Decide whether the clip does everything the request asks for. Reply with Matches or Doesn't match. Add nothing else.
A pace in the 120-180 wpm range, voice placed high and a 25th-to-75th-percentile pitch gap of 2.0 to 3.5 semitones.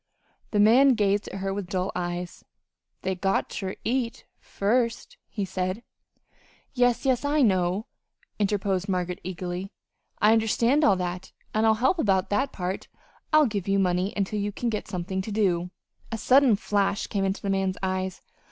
Matches